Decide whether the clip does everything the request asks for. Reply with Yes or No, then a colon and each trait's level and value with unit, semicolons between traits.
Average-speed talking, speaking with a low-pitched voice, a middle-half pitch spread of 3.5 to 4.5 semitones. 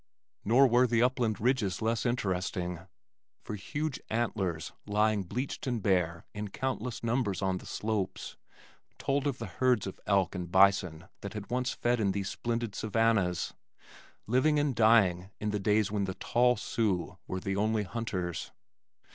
Yes: average, 155 wpm; low, 105 Hz; average, 3.9 semitones